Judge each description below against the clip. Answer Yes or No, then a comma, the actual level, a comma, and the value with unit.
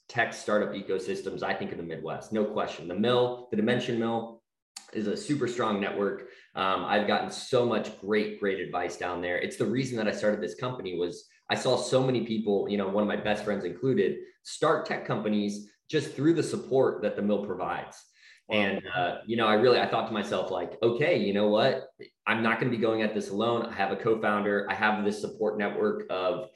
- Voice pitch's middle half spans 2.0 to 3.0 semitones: Yes, narrow, 2.4 semitones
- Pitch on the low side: Yes, low, 105 Hz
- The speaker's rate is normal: No, fast, 220 wpm